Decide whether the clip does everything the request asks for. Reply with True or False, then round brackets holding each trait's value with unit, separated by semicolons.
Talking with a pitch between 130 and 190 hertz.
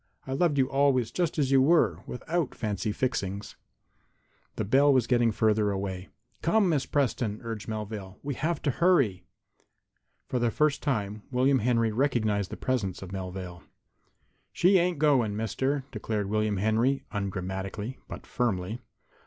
False (115 Hz)